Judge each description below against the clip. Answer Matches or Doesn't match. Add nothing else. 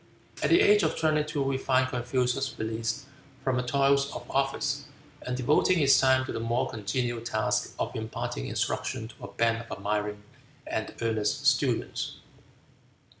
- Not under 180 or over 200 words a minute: Doesn't match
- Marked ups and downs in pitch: Doesn't match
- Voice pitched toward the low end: Matches